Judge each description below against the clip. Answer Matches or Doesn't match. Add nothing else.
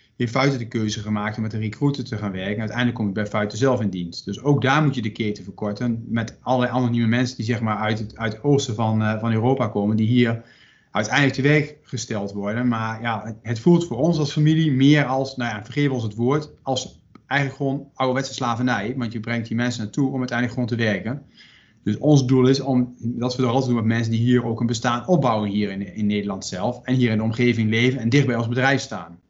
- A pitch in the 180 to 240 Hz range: Doesn't match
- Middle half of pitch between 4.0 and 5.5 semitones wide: Doesn't match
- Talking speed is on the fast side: Matches